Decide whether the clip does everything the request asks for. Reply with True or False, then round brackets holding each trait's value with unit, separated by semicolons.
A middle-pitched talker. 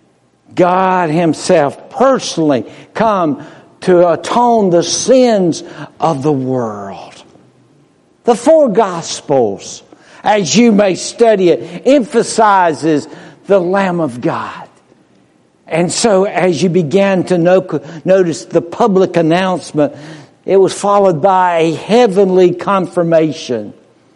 True (180 Hz)